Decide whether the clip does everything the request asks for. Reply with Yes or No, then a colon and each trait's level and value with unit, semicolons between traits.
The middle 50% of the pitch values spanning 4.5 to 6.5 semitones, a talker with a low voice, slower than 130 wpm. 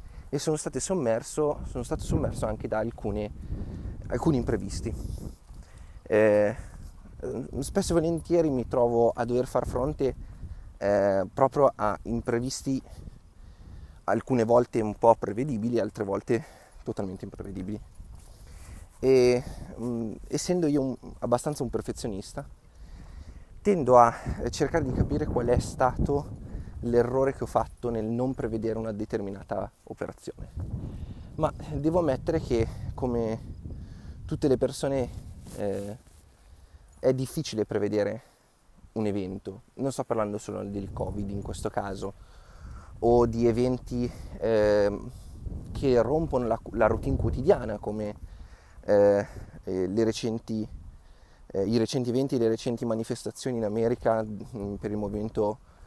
No: average, 4.0 semitones; low, 110 Hz; average, 120 wpm